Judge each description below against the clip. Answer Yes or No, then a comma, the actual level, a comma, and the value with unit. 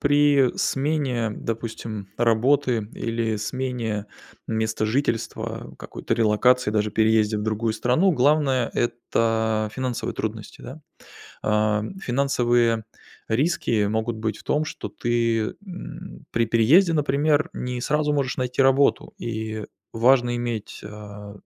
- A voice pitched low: Yes, low, 115 Hz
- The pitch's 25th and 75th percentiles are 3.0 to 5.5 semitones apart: Yes, average, 3.5 semitones